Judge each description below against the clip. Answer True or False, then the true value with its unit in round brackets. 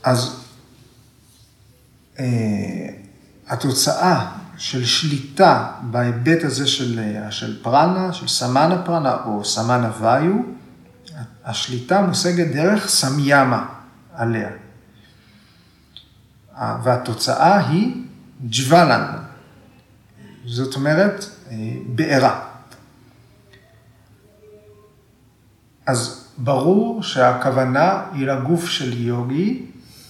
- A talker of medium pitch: False (125 Hz)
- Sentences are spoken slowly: True (75 wpm)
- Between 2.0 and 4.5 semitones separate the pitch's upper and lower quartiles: True (4.1 semitones)